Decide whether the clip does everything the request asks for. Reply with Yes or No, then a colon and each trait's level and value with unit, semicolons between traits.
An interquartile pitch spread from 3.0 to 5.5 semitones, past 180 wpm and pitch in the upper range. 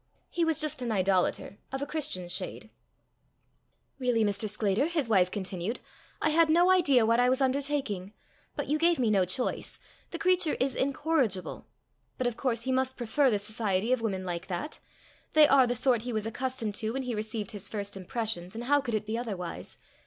Yes: average, 5.0 semitones; average, 195 wpm; high, 235 Hz